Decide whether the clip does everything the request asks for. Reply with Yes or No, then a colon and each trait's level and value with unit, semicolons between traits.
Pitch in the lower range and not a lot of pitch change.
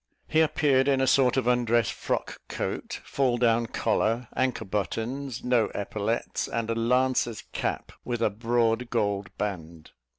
Yes: low, 120 Hz; narrow, 2.3 semitones